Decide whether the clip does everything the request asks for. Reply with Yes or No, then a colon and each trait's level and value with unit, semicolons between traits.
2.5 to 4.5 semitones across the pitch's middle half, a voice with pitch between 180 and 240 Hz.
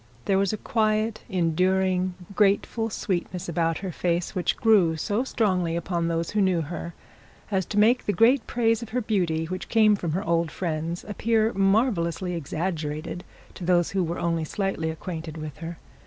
Yes: average, 3.9 semitones; medium, 185 Hz